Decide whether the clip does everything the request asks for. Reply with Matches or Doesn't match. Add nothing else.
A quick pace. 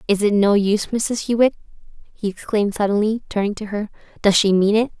Doesn't match